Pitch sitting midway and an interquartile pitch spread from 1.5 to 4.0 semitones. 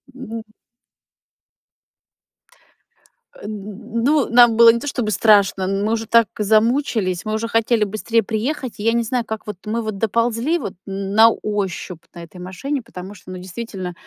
No: high, 220 Hz; average, 2.9 semitones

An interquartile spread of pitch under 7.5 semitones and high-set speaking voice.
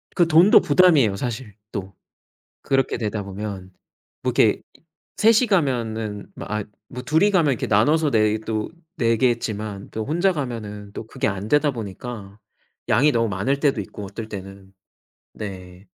No: wide, 5.5 semitones; low, 110 Hz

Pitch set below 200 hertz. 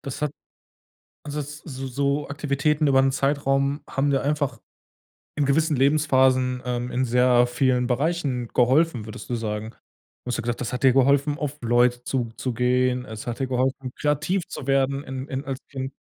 Yes: low, 135 Hz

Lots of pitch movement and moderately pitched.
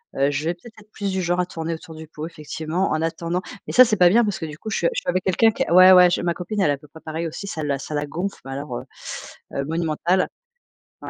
No: average, 3.1 semitones; medium, 170 Hz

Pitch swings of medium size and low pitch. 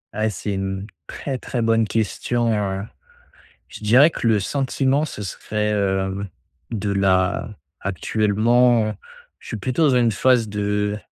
Yes: average, 3.1 semitones; low, 105 Hz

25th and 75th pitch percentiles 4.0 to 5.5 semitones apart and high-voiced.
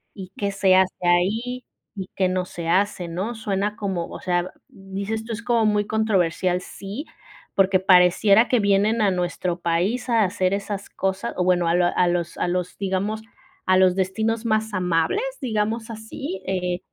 No: average, 3.2 semitones; high, 195 Hz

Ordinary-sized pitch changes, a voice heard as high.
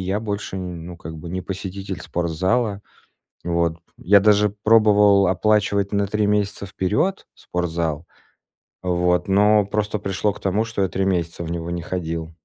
No: average, 3.0 semitones; very low, 95 Hz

